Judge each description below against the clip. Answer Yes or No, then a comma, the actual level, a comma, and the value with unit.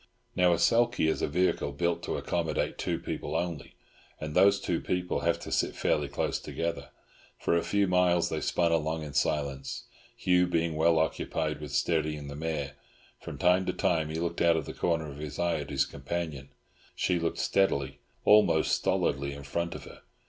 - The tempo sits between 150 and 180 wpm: No, average, 190 wpm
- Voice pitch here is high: No, very low, 80 Hz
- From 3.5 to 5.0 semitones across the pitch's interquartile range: No, average, 2.9 semitones